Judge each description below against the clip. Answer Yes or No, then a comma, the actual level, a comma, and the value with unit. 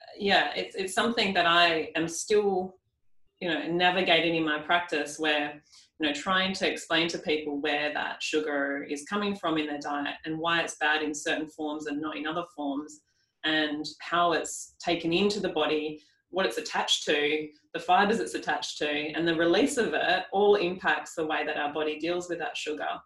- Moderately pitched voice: Yes, medium, 155 Hz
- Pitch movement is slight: Yes, narrow, 2.3 semitones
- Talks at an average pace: Yes, average, 195 wpm